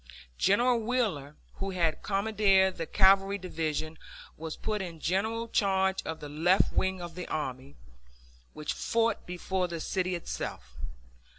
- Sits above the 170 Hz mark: Yes, medium, 185 Hz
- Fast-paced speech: No, slow, 135 wpm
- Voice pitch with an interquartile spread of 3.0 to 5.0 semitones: Yes, average, 3.7 semitones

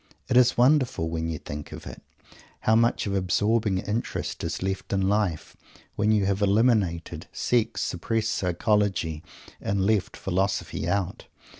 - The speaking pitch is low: Yes, low, 100 Hz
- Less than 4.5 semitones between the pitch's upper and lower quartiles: Yes, average, 3.4 semitones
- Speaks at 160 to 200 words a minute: No, average, 145 wpm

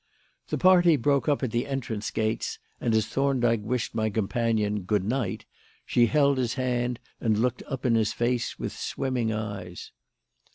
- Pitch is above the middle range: No, low, 120 Hz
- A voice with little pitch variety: No, average, 3.2 semitones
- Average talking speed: Yes, average, 165 wpm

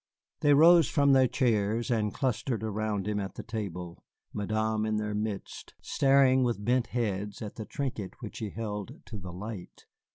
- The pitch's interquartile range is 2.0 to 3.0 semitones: No, average, 3.4 semitones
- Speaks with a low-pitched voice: Yes, low, 110 Hz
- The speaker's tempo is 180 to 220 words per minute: No, average, 170 wpm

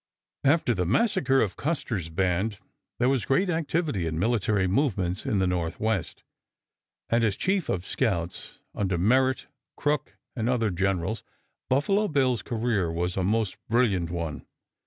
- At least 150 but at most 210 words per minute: No, average, 140 wpm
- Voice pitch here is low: Yes, low, 110 Hz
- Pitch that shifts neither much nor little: No, wide, 6.6 semitones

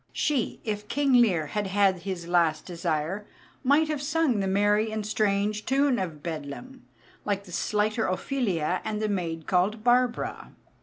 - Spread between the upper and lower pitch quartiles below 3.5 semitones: No, average, 5.2 semitones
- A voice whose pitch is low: No, high, 205 Hz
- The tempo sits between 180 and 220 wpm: No, average, 155 wpm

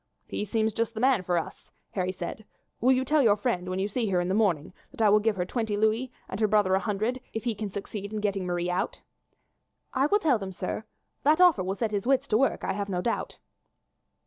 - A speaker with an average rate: No, fast, 245 wpm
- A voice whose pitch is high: Yes, high, 210 Hz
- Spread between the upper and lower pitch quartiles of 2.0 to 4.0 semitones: Yes, average, 3.7 semitones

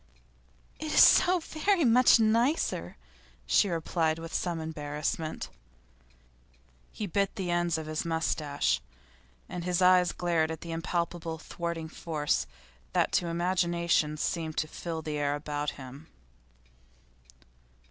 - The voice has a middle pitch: Yes, medium, 165 Hz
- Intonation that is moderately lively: No, narrow, 2.3 semitones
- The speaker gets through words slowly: Yes, slow, 125 wpm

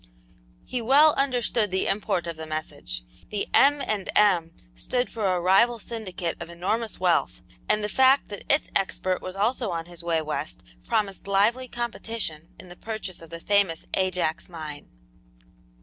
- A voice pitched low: No, high, 195 Hz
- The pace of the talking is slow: No, average, 165 wpm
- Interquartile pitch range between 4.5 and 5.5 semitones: Yes, average, 5.0 semitones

